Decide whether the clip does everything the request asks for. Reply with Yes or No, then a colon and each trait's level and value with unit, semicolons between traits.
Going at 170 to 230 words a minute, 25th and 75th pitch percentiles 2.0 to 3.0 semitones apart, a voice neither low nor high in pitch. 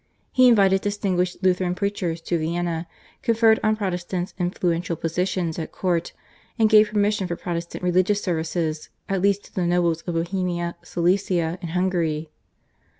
No: average, 145 wpm; narrow, 2.5 semitones; medium, 180 Hz